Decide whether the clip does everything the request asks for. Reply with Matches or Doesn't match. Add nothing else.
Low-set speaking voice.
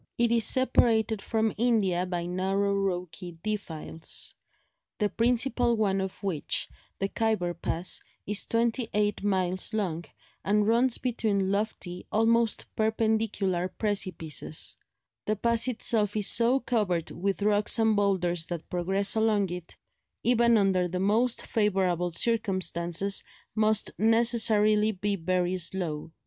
Doesn't match